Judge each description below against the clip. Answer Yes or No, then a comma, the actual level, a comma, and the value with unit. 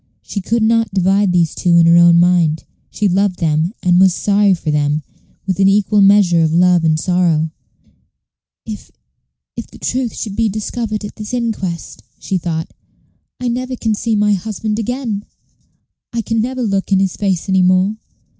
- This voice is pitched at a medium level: No, high, 195 Hz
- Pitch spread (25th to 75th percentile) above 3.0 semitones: Yes, average, 3.7 semitones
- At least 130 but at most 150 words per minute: No, average, 185 wpm